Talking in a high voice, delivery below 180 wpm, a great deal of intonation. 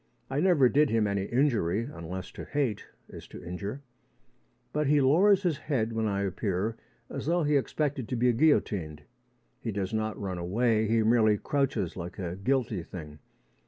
No: low, 115 Hz; average, 170 wpm; wide, 6.1 semitones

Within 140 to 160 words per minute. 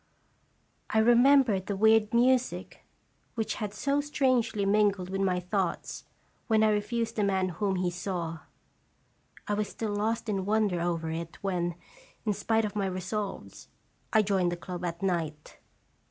Yes: average, 155 wpm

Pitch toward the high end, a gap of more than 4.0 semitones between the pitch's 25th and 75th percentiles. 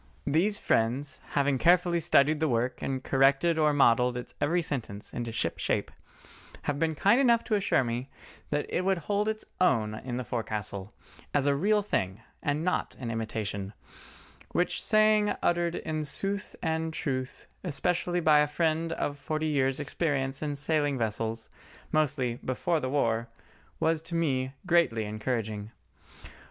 No: medium, 145 Hz; wide, 5.5 semitones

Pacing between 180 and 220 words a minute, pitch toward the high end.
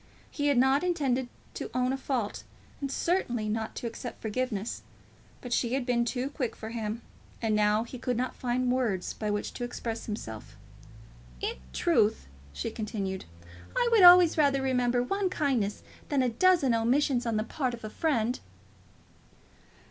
No: average, 165 wpm; high, 245 Hz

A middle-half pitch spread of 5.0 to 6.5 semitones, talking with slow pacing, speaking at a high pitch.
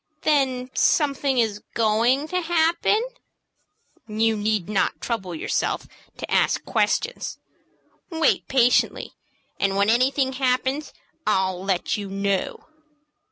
Yes: average, 5.3 semitones; slow, 110 wpm; high, 245 Hz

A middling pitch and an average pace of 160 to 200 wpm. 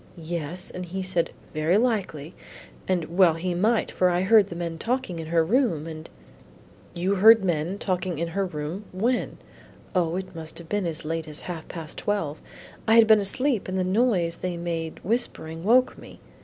Yes: medium, 180 Hz; average, 190 wpm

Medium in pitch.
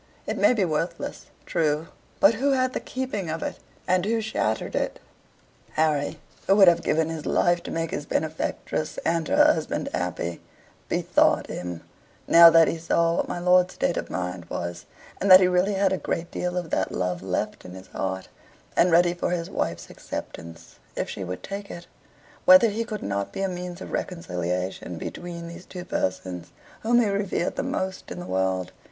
Yes: medium, 170 Hz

